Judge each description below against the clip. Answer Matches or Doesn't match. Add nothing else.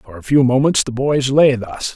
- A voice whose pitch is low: Matches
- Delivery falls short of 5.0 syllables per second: Matches